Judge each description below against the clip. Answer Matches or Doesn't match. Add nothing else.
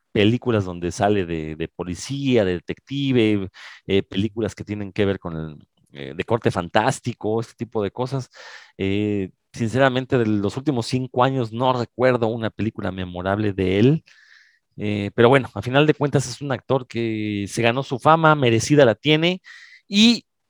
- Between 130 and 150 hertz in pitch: Doesn't match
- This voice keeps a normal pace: Matches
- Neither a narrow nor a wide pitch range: Matches